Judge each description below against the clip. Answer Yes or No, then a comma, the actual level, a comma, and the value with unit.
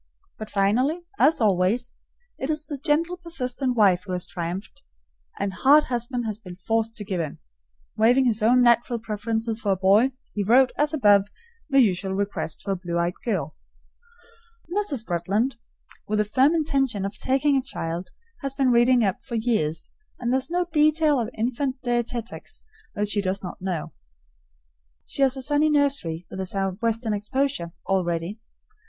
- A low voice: No, high, 230 Hz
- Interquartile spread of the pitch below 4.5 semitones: No, wide, 5.4 semitones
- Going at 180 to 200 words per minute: No, average, 170 wpm